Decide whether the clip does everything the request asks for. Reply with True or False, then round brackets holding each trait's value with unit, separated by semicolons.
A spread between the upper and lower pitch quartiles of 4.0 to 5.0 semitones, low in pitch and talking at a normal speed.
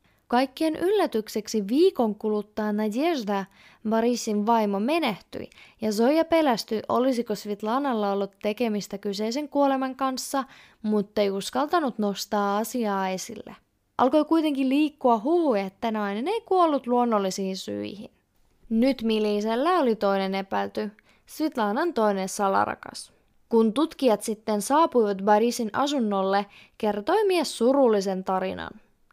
False (4.6 semitones; 225 Hz; 105 wpm)